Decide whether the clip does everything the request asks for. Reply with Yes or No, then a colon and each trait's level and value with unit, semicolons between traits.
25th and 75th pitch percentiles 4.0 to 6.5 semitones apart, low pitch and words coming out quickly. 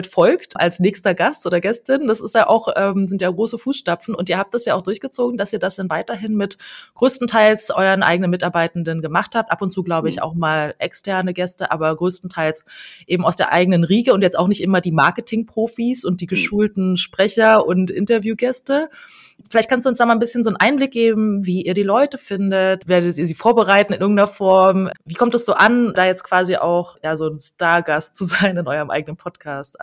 No: average, 4.3 semitones; high, 195 Hz; fast, 215 wpm